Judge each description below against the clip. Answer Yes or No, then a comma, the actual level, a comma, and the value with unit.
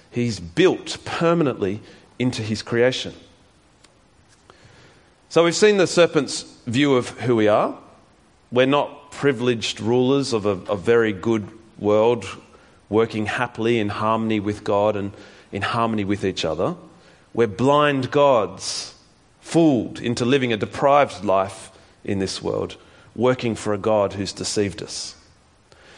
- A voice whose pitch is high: No, low, 115 Hz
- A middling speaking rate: No, slow, 130 wpm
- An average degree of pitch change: Yes, average, 3.7 semitones